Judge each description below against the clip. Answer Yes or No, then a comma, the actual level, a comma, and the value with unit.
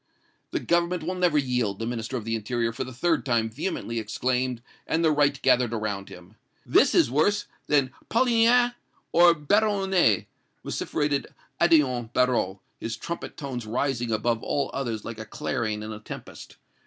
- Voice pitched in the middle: No, low, 125 Hz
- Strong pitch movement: Yes, wide, 6.2 semitones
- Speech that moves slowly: No, average, 160 wpm